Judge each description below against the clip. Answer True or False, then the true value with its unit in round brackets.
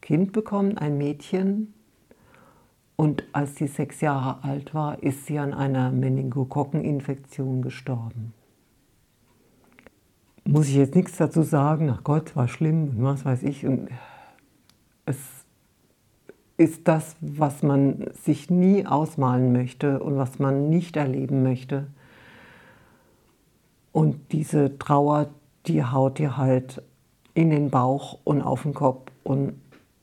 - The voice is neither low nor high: True (145 Hz)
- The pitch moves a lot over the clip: False (2.6 semitones)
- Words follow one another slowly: True (120 wpm)